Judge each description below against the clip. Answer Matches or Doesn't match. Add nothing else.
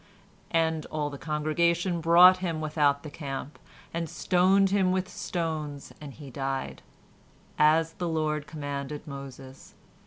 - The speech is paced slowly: Matches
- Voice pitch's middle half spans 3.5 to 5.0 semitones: Doesn't match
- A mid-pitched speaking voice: Matches